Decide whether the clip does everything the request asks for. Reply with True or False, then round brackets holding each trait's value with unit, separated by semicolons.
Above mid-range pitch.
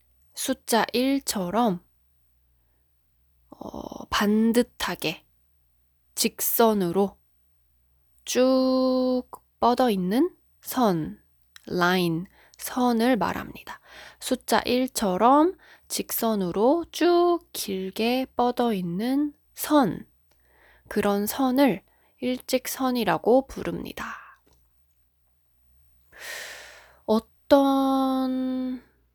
True (225 Hz)